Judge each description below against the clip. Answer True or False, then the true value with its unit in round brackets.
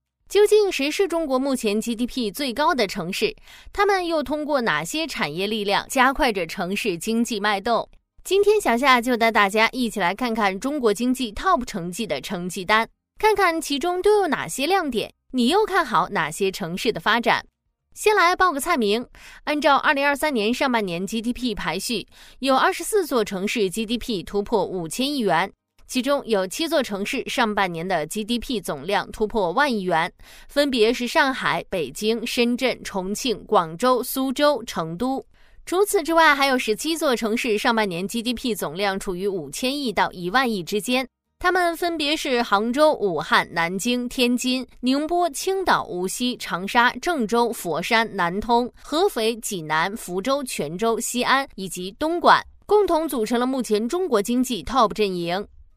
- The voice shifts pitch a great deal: True (5.7 semitones)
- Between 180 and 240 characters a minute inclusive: False (265 characters per minute)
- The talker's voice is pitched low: False (240 Hz)